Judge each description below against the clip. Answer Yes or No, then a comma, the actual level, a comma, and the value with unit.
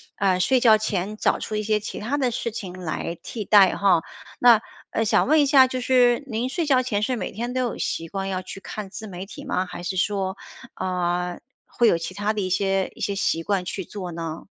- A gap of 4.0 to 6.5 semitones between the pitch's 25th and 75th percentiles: Yes, average, 4.3 semitones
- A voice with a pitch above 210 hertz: No, high, 205 Hz